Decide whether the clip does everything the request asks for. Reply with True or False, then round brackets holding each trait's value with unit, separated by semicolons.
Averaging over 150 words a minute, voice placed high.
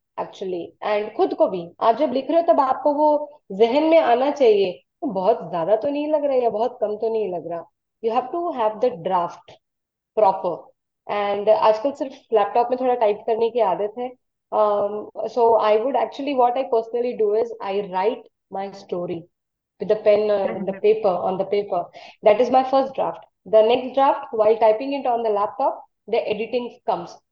True (180 wpm; 225 Hz)